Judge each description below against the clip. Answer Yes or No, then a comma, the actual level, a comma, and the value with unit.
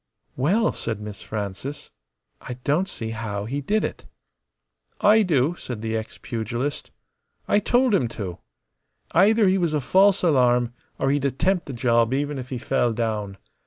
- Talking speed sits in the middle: Yes, average, 160 wpm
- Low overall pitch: Yes, low, 130 Hz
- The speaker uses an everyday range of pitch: No, wide, 7.6 semitones